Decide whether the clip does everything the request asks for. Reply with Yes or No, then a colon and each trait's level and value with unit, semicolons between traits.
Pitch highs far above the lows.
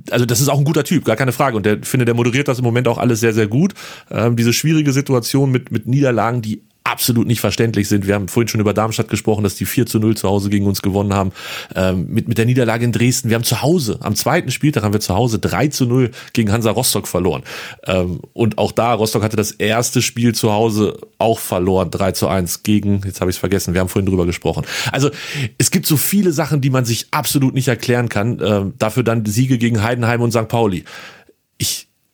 No: average, 3.4 semitones